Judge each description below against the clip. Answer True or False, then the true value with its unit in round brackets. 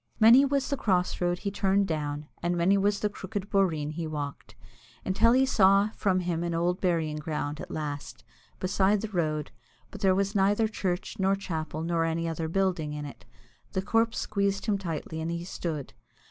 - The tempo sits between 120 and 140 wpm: False (190 wpm)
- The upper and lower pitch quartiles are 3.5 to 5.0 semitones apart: True (3.8 semitones)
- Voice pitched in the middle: True (180 Hz)